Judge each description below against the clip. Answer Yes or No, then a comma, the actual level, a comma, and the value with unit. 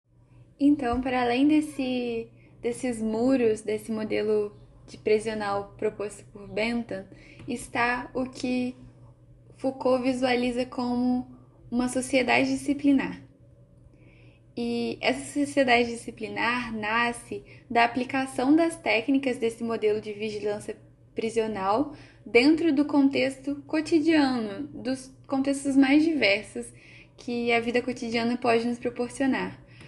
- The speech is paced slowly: Yes, slow, 100 wpm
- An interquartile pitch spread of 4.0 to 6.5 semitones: No, average, 3.5 semitones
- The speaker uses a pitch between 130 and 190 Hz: No, high, 240 Hz